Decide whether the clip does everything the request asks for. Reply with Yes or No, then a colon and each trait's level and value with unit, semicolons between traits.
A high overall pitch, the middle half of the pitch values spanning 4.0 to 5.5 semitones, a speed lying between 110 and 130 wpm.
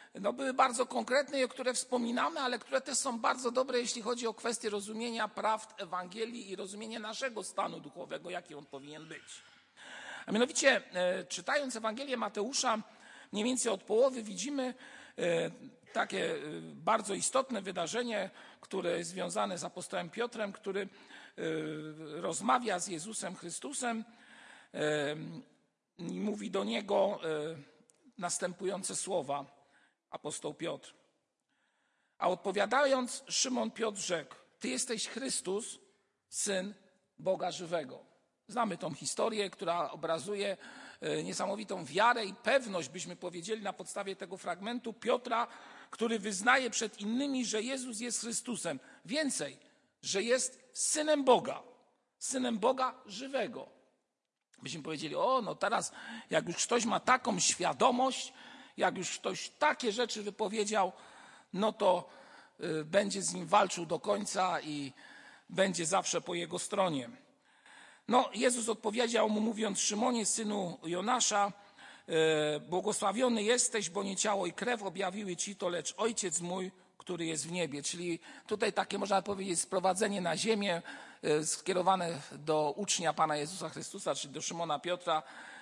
Yes: high, 205 Hz; average, 5.1 semitones; average, 125 wpm